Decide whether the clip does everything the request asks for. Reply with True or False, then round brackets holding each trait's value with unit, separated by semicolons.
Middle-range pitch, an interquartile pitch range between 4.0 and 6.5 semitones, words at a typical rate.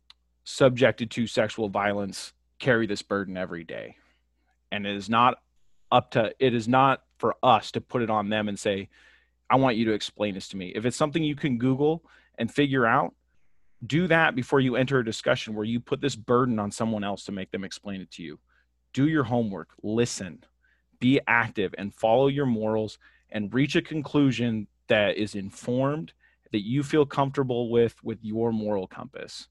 False (115 Hz; 4.3 semitones; 185 wpm)